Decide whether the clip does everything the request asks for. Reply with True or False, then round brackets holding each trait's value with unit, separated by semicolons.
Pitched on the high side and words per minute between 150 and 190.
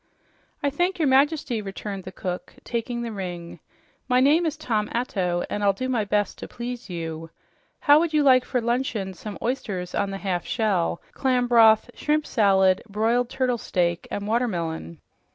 True (220 Hz; 170 wpm)